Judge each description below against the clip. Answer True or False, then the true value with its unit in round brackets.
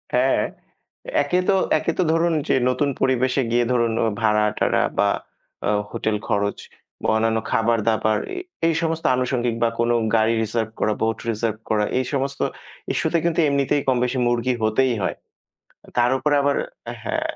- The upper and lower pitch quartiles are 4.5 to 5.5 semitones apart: False (3.7 semitones)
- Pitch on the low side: True (120 Hz)